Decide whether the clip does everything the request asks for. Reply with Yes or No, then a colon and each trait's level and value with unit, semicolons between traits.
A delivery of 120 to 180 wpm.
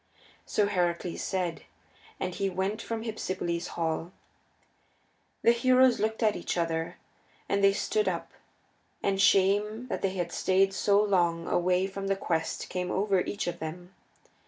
Yes: average, 150 wpm